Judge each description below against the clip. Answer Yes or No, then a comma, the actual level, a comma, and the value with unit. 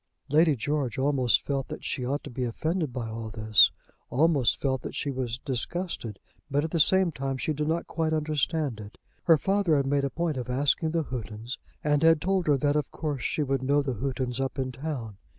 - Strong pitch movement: No, average, 3.7 semitones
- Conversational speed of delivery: No, fast, 215 wpm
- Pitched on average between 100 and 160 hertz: Yes, medium, 140 Hz